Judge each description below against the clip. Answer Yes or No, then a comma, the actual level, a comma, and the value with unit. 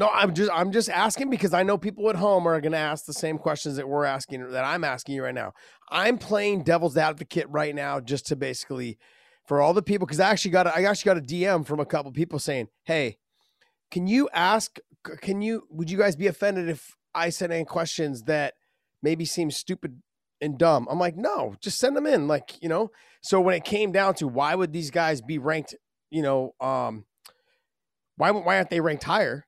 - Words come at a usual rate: No, fast, 220 wpm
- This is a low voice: No, medium, 165 Hz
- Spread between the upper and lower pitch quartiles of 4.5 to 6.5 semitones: Yes, average, 5.0 semitones